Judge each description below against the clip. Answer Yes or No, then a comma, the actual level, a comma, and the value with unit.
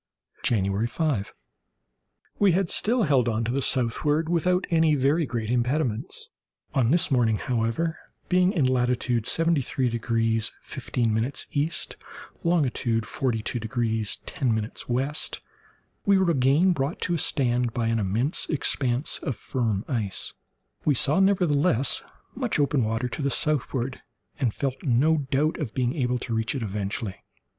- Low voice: Yes, low, 130 Hz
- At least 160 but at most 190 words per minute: No, average, 140 wpm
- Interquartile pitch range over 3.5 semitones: Yes, average, 4.9 semitones